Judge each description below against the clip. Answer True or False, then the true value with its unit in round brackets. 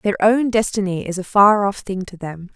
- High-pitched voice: True (200 Hz)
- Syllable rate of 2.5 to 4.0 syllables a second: False (4.9 syllables/s)